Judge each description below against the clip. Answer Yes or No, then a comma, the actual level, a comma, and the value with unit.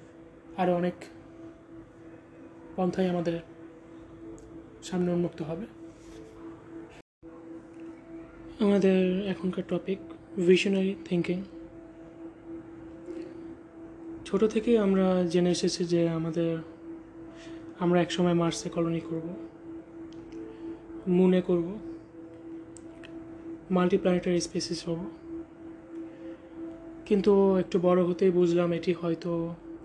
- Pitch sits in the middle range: Yes, medium, 180 Hz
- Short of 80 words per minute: Yes, average, 70 wpm